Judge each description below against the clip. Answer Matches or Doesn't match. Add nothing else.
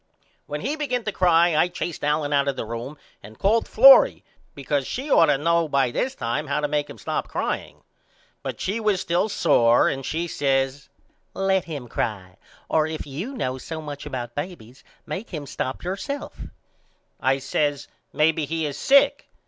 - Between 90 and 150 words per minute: Doesn't match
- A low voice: Doesn't match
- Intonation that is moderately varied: Matches